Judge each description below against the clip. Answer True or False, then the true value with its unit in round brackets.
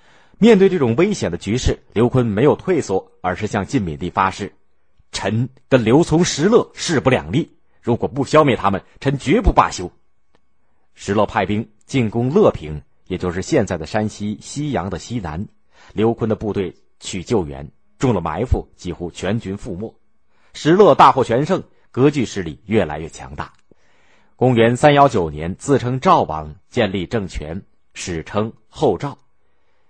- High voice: False (105 Hz)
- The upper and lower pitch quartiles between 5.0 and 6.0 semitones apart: True (5.3 semitones)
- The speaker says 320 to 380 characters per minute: False (235 characters per minute)